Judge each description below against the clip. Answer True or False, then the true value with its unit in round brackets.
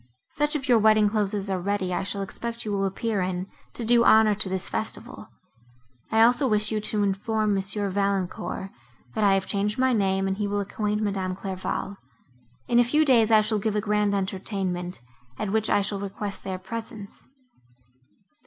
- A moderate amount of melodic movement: False (2.2 semitones)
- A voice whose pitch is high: True (205 Hz)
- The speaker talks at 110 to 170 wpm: False (190 wpm)